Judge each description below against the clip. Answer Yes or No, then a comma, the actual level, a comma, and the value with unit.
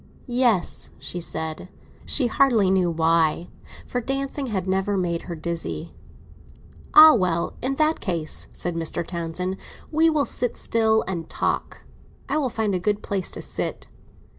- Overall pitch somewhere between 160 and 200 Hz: Yes, high, 190 Hz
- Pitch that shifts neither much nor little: No, wide, 6.4 semitones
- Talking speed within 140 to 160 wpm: Yes, average, 150 wpm